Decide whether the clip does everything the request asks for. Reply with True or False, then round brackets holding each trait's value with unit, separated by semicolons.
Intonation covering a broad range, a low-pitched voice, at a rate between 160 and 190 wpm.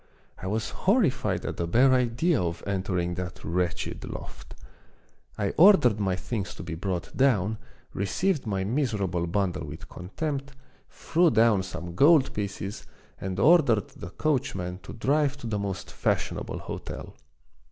False (6.8 semitones; 100 Hz; 140 wpm)